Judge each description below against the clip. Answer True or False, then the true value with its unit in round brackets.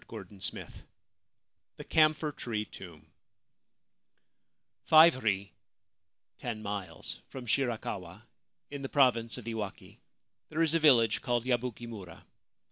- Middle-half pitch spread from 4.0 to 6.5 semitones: True (4.7 semitones)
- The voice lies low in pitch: True (115 Hz)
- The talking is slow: True (115 wpm)